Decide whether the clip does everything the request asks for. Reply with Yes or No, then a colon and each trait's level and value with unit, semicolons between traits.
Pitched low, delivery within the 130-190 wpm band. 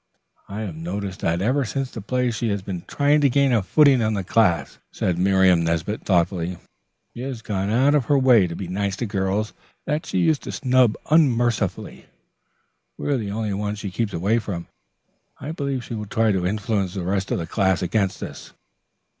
No: low, 105 Hz; average, 200 wpm